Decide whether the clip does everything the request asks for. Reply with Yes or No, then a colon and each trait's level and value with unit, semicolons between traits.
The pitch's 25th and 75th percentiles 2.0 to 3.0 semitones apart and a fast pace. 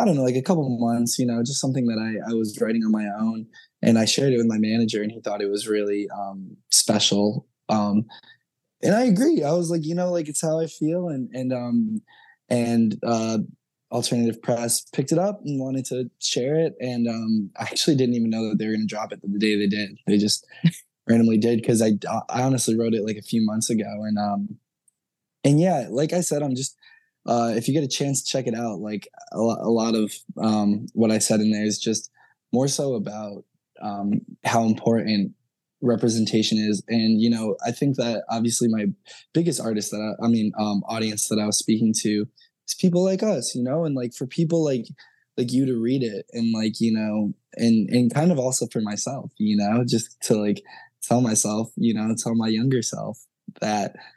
No: average, 3.7 semitones; fast, 220 wpm